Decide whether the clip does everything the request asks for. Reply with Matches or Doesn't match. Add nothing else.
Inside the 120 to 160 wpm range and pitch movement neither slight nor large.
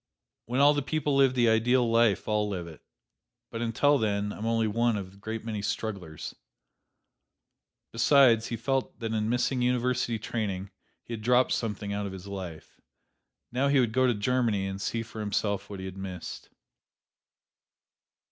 Doesn't match